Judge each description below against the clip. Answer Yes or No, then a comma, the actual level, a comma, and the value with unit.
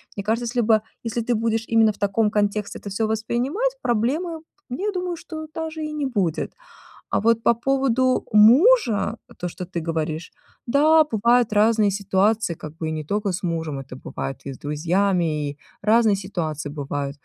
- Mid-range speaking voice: No, high, 215 Hz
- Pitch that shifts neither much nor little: No, wide, 5.9 semitones